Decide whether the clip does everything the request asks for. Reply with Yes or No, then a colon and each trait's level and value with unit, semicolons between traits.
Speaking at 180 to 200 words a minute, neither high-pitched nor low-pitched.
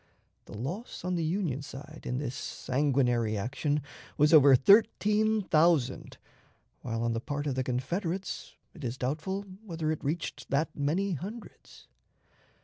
No: average, 145 wpm; medium, 150 Hz